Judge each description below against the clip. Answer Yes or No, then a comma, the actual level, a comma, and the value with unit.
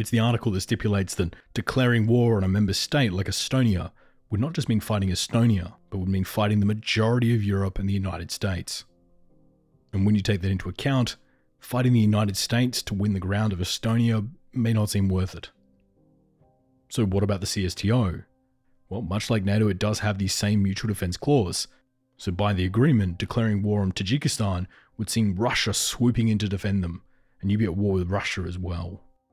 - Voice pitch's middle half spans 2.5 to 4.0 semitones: Yes, average, 3.4 semitones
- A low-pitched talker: Yes, low, 105 Hz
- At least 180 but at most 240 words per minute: Yes, average, 195 wpm